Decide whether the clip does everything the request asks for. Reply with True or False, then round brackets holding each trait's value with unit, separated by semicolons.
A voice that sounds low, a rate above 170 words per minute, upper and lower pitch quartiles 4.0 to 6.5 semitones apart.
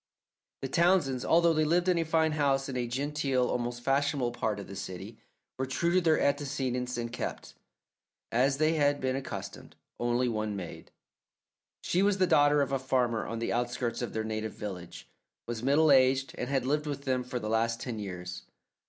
False (130 Hz; 190 wpm; 3.6 semitones)